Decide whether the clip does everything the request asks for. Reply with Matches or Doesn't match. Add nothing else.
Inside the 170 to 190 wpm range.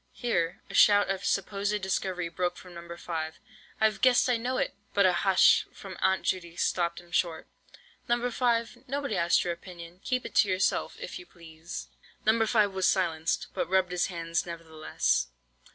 Matches